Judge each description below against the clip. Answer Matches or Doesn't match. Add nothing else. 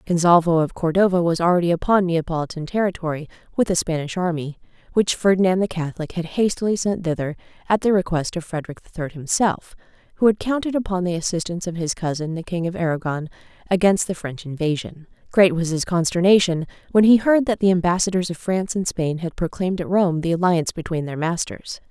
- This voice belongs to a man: Doesn't match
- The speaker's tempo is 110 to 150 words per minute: Doesn't match